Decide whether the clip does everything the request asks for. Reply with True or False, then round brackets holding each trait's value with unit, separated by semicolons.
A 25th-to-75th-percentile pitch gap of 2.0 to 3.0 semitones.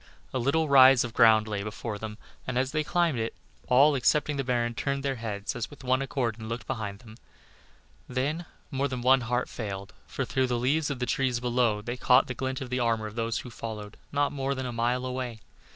True (2.7 semitones)